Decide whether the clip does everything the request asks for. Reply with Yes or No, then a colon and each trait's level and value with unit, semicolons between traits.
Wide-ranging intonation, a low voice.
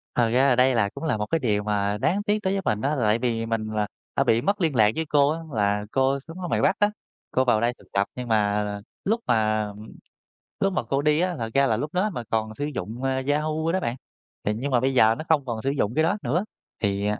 Yes: wide, 6.0 semitones; low, 125 Hz